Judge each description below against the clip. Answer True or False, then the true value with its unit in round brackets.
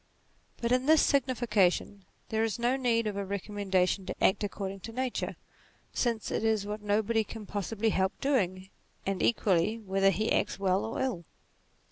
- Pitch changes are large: False (2.9 semitones)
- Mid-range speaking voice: False (210 Hz)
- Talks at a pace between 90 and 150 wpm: False (165 wpm)